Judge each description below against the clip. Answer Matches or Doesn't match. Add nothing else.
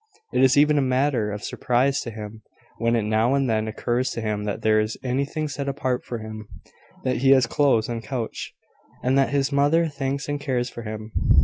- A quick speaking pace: Matches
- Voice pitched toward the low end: Matches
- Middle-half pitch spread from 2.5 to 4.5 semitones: Matches